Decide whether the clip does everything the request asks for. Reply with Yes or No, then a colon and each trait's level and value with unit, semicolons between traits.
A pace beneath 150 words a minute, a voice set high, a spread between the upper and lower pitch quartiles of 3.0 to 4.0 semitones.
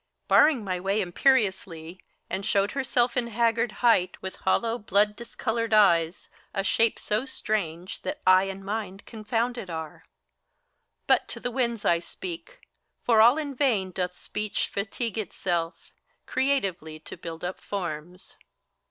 No: average, 140 wpm; high, 210 Hz; average, 4.4 semitones